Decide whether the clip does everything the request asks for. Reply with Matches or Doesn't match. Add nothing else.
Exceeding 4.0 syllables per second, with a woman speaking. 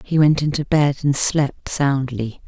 Doesn't match